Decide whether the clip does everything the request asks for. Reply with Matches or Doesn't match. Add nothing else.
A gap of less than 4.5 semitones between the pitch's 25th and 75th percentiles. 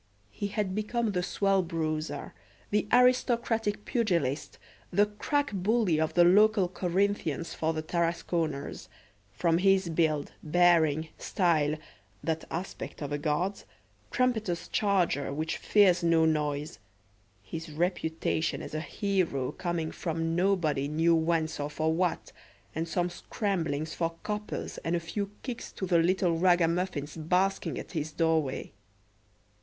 Matches